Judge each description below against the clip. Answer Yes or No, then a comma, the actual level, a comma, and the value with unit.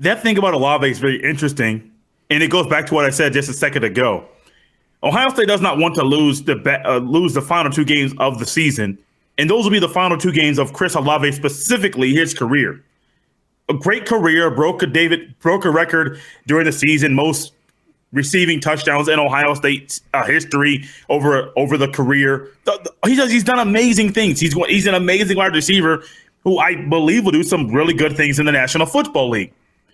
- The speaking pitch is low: No, medium, 155 Hz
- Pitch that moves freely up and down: No, average, 3.9 semitones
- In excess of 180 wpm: Yes, fast, 205 wpm